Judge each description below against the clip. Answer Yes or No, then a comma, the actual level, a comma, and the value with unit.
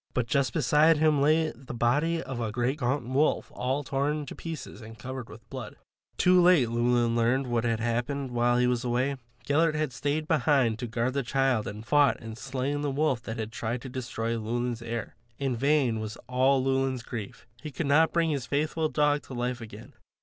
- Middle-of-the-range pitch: No, low, 130 Hz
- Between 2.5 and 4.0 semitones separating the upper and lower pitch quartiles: Yes, average, 3.5 semitones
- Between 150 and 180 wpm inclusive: No, fast, 205 wpm